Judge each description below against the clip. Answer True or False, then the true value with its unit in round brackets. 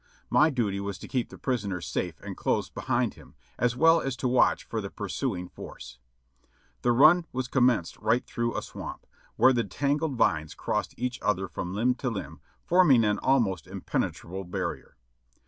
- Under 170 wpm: False (175 wpm)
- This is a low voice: True (115 Hz)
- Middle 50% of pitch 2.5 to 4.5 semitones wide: False (5.3 semitones)